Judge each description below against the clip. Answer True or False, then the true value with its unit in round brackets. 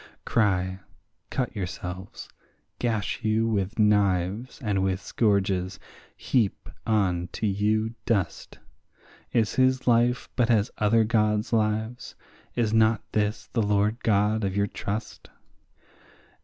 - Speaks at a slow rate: True (115 wpm)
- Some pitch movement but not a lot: False (2.3 semitones)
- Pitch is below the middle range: True (105 Hz)